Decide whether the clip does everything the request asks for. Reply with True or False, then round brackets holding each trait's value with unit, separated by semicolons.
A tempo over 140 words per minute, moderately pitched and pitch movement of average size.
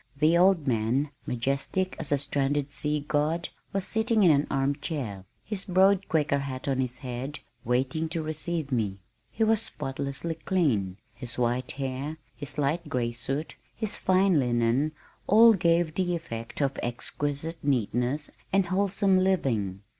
True (150 wpm; 145 Hz; 5.0 semitones)